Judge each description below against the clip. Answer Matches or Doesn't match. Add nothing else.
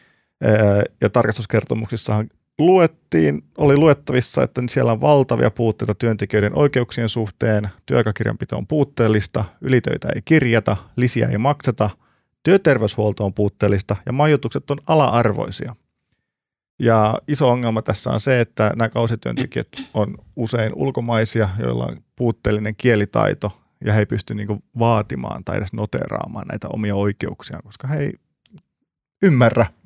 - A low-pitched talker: Matches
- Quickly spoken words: Doesn't match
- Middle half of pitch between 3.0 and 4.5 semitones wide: Matches